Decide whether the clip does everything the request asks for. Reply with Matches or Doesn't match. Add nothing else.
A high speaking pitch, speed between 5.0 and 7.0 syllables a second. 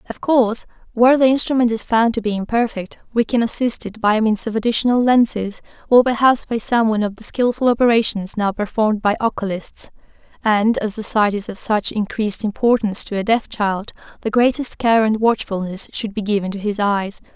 Matches